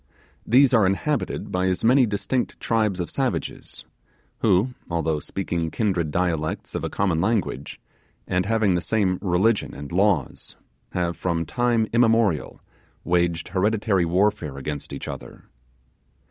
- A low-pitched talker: Yes, very low, 95 Hz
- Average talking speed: No, slow, 130 wpm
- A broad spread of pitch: No, average, 4.6 semitones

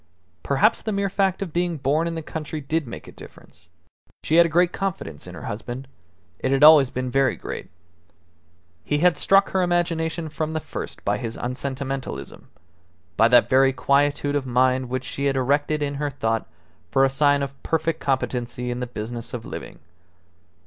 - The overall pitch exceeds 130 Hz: Yes, medium, 140 Hz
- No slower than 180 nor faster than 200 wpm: Yes, average, 185 wpm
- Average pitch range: Yes, average, 4.0 semitones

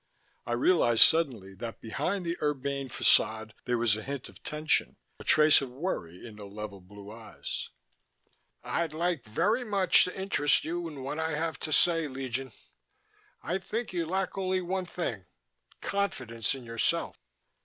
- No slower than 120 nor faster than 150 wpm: No, average, 160 wpm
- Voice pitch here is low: No, medium, 145 Hz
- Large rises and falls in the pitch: Yes, wide, 7.1 semitones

